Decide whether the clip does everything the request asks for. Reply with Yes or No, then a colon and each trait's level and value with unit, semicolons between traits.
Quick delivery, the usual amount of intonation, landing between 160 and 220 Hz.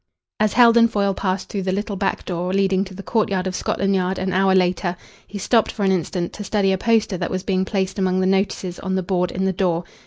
No: fast, 245 wpm; narrow, 1.3 semitones; high, 190 Hz